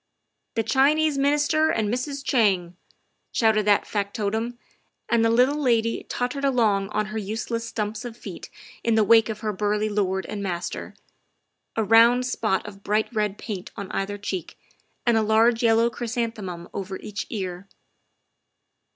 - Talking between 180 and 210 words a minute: No, average, 155 wpm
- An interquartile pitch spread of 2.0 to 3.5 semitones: Yes, average, 2.8 semitones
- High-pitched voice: Yes, high, 220 Hz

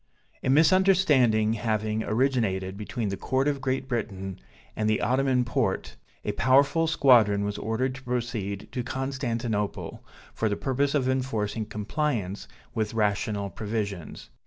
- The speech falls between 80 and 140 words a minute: Yes, slow, 135 wpm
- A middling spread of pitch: Yes, average, 4.0 semitones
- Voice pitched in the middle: No, low, 115 Hz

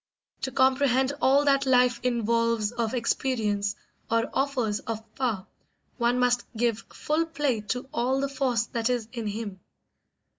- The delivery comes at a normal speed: Yes, average, 145 wpm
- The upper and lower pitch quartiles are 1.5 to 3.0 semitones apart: Yes, average, 2.7 semitones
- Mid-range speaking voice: No, high, 245 Hz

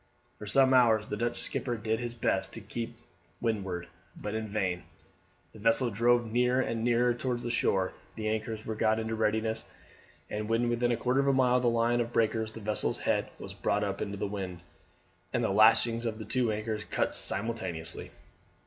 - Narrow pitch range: Yes, narrow, 2.0 semitones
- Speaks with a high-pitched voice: No, low, 110 Hz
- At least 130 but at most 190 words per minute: No, average, 200 wpm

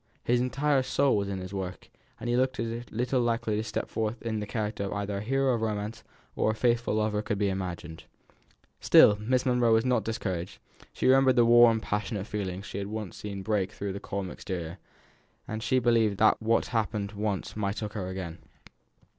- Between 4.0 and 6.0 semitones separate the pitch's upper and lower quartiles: No, average, 3.0 semitones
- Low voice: Yes, low, 110 Hz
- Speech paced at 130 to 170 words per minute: No, fast, 205 wpm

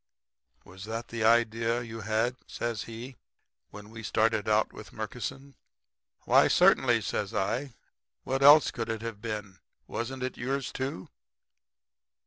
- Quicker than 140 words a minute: No, slow, 135 wpm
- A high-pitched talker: No, low, 115 Hz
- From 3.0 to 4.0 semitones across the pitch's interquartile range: No, narrow, 2.6 semitones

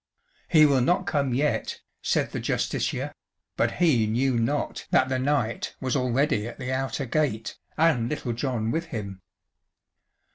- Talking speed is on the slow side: No, average, 150 wpm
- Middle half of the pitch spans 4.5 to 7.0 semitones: No, average, 4.0 semitones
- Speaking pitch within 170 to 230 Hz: No, low, 130 Hz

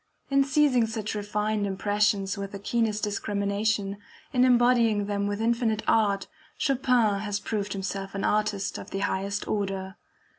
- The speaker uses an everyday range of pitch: No, narrow, 2.0 semitones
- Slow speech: No, average, 145 wpm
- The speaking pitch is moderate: No, high, 210 Hz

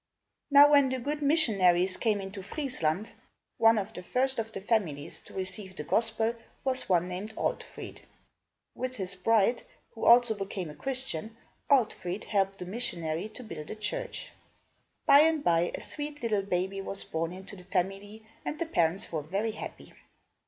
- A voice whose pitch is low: No, high, 205 Hz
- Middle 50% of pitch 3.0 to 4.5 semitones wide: No, average, 5.1 semitones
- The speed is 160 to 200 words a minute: Yes, average, 165 wpm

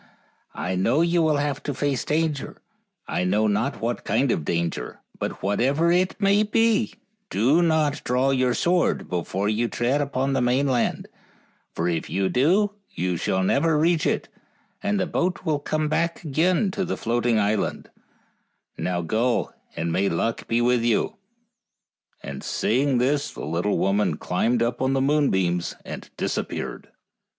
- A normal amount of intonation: No, wide, 6.9 semitones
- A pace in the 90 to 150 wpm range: No, average, 160 wpm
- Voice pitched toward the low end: Yes, low, 130 Hz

